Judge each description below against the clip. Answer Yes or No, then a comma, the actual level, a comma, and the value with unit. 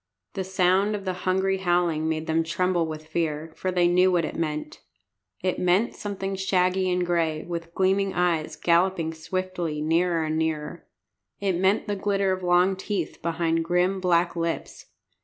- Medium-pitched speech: Yes, medium, 175 Hz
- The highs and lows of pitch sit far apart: No, narrow, 2.4 semitones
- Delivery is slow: No, average, 165 wpm